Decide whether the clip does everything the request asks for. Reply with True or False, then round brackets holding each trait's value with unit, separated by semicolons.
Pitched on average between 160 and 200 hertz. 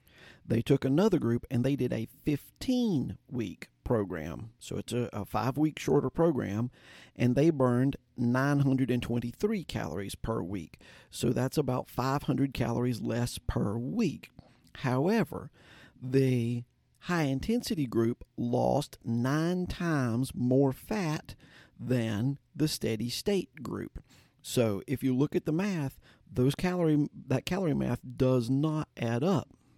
False (130 Hz)